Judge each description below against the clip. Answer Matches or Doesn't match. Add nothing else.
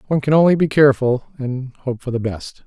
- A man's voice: Matches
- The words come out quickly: Matches